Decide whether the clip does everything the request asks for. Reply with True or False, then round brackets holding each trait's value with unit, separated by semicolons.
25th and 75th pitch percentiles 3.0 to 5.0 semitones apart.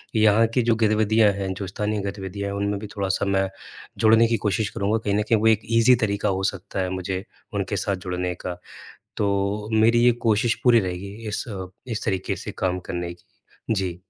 False (2.4 semitones)